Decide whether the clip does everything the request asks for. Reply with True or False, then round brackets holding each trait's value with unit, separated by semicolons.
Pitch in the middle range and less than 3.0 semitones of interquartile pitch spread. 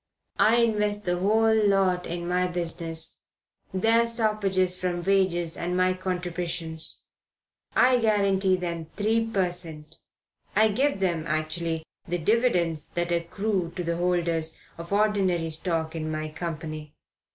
False (180 Hz; 3.5 semitones)